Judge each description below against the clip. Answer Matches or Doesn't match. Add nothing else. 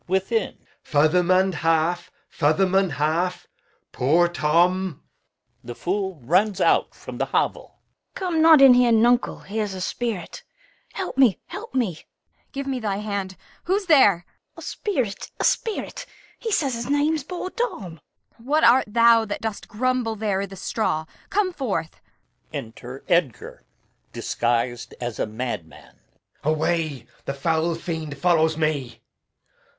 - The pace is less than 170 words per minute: Matches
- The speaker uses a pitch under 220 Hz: Matches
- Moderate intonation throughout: Doesn't match